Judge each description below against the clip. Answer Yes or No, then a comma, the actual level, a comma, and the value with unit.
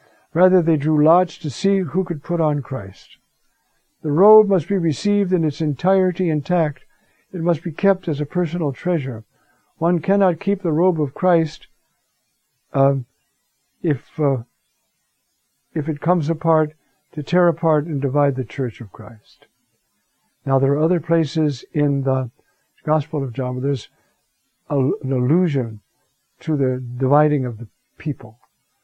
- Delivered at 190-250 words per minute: No, average, 150 wpm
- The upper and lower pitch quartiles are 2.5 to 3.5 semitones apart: No, average, 4.2 semitones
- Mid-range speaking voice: Yes, medium, 155 Hz